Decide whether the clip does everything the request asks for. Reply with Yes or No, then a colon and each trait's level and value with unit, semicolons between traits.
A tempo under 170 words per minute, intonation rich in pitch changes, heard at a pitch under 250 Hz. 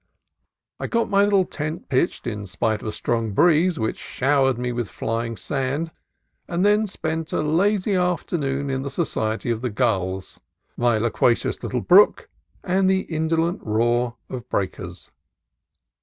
Yes: average, 155 wpm; wide, 6.9 semitones; low, 135 Hz